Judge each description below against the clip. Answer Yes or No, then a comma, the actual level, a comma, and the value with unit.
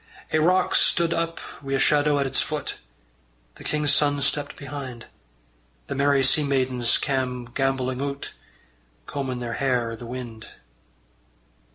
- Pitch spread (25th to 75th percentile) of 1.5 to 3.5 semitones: Yes, narrow, 2.4 semitones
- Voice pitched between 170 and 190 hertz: No, low, 135 Hz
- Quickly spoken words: No, average, 145 wpm